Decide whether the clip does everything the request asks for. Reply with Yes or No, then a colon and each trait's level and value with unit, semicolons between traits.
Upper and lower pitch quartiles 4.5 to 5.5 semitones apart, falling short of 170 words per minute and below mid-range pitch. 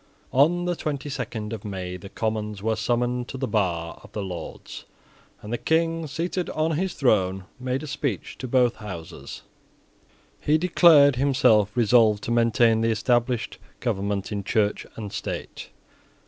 Yes: average, 5.1 semitones; average, 155 wpm; low, 115 Hz